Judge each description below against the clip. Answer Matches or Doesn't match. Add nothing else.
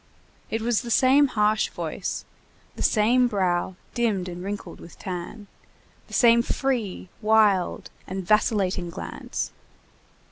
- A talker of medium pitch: Doesn't match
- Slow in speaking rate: Matches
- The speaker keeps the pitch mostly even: Doesn't match